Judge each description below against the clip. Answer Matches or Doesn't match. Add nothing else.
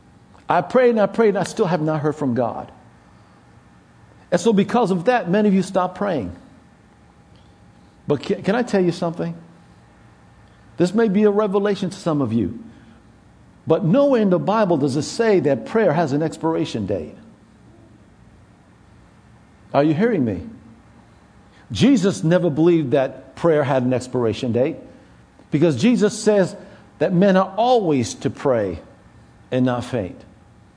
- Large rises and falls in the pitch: Matches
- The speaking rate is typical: Matches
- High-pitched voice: Doesn't match